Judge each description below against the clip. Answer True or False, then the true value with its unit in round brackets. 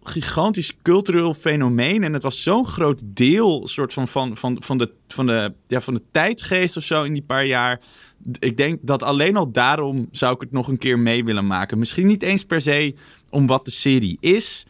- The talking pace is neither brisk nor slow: False (210 wpm)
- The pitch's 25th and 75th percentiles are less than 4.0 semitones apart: False (4.4 semitones)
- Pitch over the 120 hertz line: True (135 Hz)